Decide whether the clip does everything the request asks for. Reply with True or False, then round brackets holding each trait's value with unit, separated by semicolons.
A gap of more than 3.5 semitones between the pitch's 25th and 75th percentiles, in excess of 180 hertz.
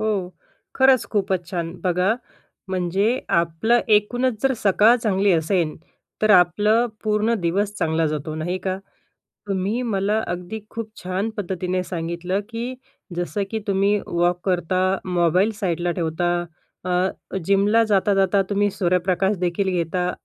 False (2.9 semitones; 190 Hz)